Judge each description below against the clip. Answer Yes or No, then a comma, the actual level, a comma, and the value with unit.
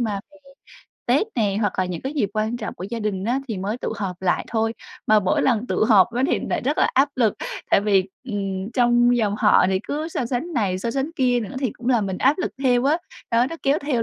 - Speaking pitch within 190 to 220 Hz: No, high, 230 Hz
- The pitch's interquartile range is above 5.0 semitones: No, average, 4.1 semitones